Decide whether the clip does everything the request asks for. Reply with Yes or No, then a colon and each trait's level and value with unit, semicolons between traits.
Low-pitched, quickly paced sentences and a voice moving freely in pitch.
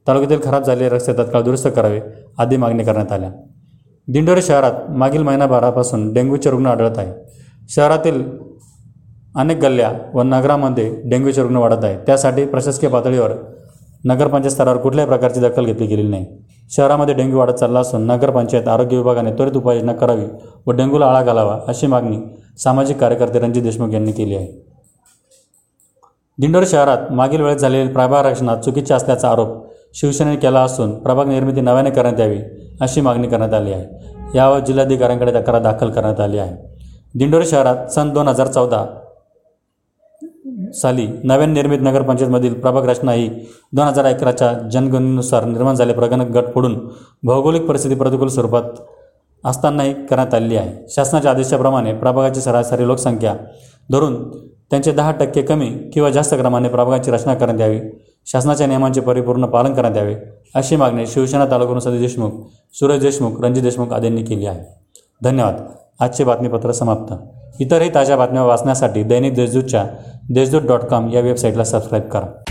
No: low, 125 Hz; fast, 145 wpm; average, 2.7 semitones